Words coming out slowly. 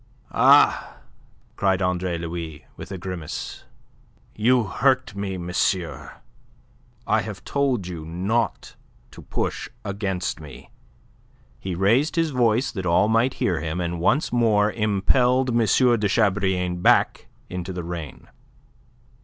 Yes: slow, 125 wpm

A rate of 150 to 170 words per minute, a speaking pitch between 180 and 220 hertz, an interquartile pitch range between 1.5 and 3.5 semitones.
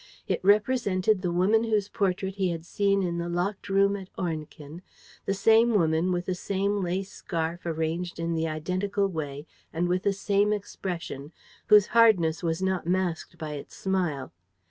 Yes: average, 165 wpm; medium, 185 Hz; average, 3.1 semitones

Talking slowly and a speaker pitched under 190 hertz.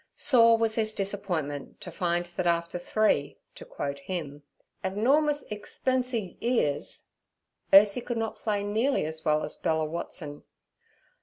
No: slow, 125 wpm; high, 195 Hz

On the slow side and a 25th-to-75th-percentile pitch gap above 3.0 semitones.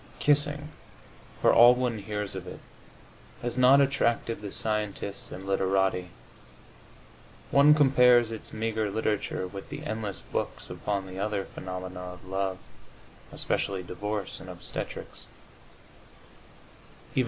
Yes: slow, 115 wpm; average, 4.0 semitones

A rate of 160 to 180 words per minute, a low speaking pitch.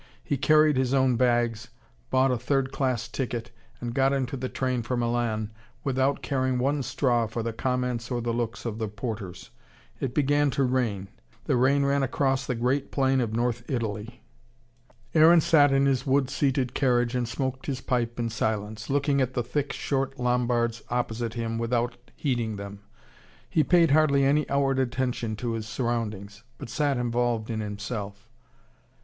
Yes: average, 170 wpm; low, 125 Hz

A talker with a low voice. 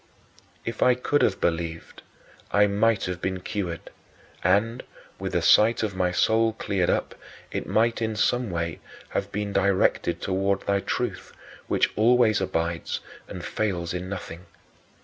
Yes: low, 100 Hz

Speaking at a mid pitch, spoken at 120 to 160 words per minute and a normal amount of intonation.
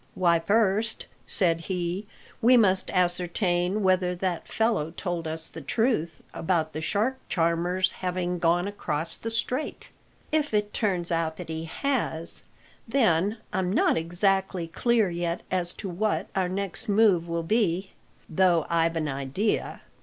Yes: medium, 180 Hz; average, 145 wpm; average, 3.6 semitones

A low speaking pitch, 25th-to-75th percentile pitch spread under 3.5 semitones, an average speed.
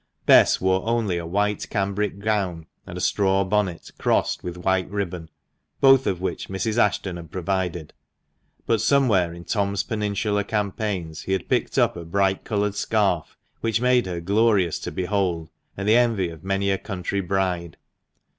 Yes: very low, 95 Hz; average, 2.7 semitones; average, 165 wpm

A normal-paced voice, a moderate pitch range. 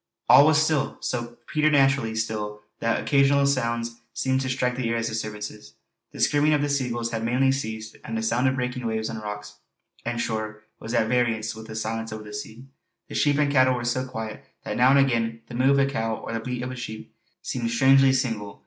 No: fast, 220 wpm; average, 3.2 semitones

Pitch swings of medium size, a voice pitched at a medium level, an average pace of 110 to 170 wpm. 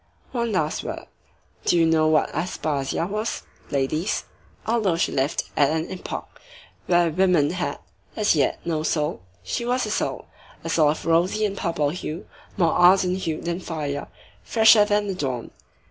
Yes: average, 3.9 semitones; medium, 170 Hz; average, 165 wpm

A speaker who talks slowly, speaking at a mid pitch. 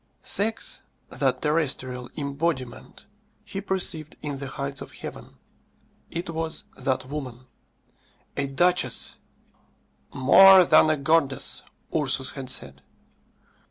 Yes: slow, 105 wpm; medium, 145 Hz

